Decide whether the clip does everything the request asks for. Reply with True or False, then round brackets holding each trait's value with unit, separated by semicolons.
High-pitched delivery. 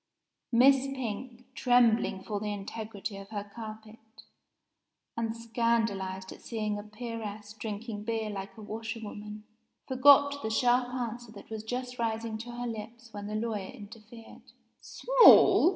True (225 Hz)